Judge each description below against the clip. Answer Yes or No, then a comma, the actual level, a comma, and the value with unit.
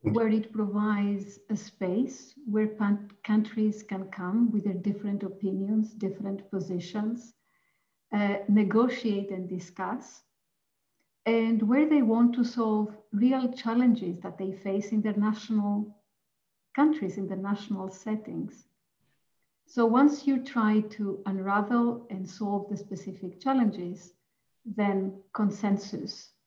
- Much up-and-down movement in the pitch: No, narrow, 2.4 semitones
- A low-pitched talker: No, high, 210 Hz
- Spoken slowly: Yes, slow, 120 wpm